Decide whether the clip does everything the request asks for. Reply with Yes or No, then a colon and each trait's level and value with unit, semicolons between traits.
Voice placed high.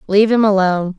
Yes: high, 200 Hz